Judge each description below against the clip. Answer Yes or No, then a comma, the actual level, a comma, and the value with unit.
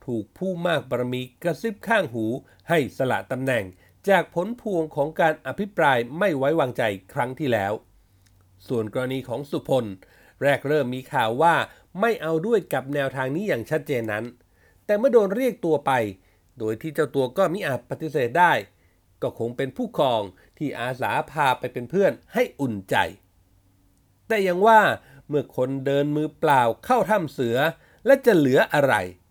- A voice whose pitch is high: No, low, 135 Hz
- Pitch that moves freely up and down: Yes, wide, 7.1 semitones